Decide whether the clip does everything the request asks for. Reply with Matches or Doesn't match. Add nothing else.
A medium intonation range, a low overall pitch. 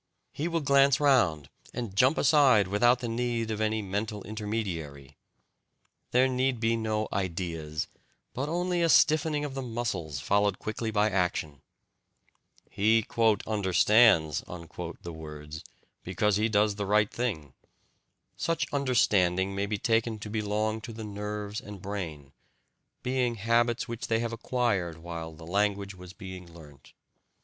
Matches